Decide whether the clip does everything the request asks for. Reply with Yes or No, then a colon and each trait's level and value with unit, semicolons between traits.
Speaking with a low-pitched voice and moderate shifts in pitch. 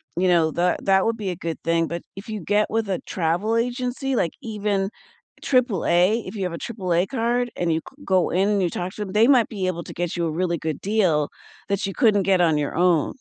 No: high, 190 Hz; average, 4.2 semitones